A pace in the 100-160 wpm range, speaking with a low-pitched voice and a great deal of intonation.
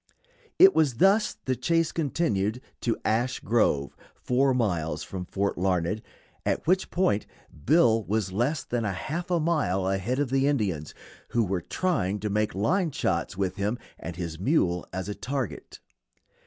Yes: average, 155 wpm; low, 110 Hz; wide, 7.1 semitones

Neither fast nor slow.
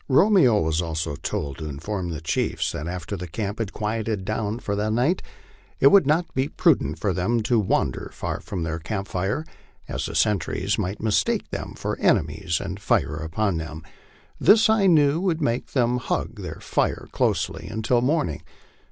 Yes: average, 180 wpm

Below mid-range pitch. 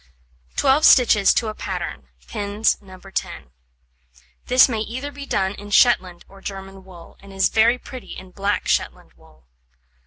No: high, 205 Hz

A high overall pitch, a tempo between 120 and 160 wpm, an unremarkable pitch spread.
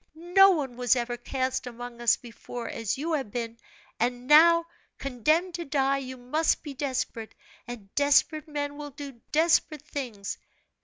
Yes: very high, 270 Hz; average, 155 wpm; average, 3.9 semitones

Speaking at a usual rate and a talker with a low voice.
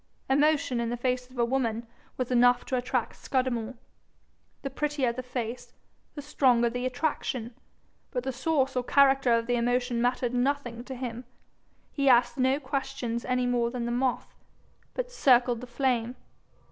No: average, 160 wpm; very high, 250 Hz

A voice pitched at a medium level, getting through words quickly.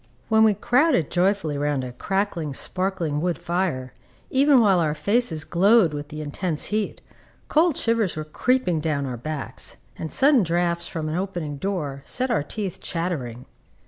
No: medium, 175 Hz; average, 160 wpm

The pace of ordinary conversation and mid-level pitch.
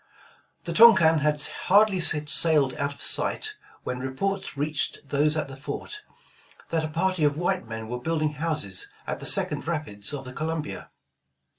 Yes: average, 160 wpm; medium, 150 Hz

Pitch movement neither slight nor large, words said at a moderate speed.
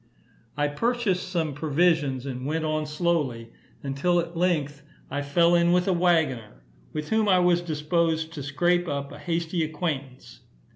Yes: average, 3.5 semitones; average, 155 wpm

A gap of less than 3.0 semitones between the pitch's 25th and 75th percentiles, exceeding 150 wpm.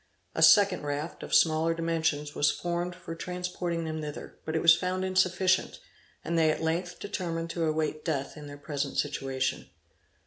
Yes: narrow, 2.6 semitones; average, 170 wpm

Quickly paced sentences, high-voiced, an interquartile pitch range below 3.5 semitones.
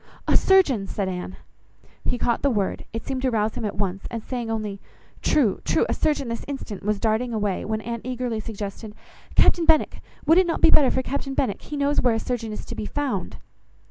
No: fast, 210 wpm; high, 230 Hz; average, 4.3 semitones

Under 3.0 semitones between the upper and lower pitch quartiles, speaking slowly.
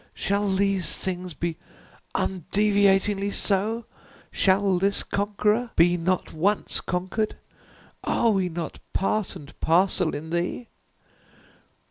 Yes: narrow, 2.4 semitones; slow, 105 wpm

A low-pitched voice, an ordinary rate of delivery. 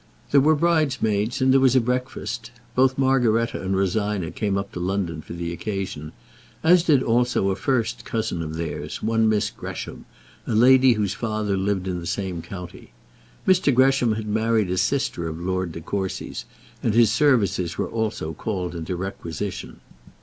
Yes: low, 105 Hz; average, 170 wpm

